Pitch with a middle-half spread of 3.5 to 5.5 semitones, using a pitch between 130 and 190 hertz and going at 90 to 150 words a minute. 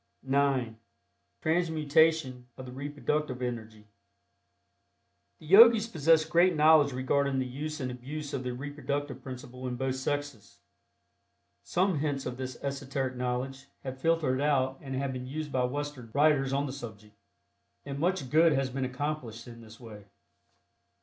No: average, 2.9 semitones; low, 135 Hz; average, 145 wpm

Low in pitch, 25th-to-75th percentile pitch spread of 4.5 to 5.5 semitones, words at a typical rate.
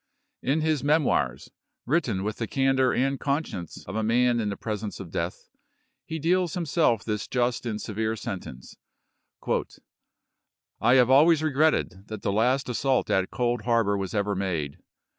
Yes: low, 120 Hz; average, 5.0 semitones; average, 160 wpm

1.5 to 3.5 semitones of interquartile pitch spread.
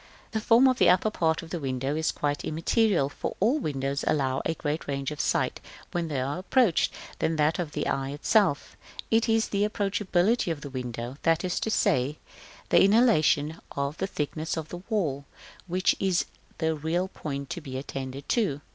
No: wide, 5.4 semitones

